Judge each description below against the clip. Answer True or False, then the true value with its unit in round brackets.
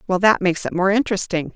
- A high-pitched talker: True (195 Hz)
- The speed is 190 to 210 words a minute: False (230 wpm)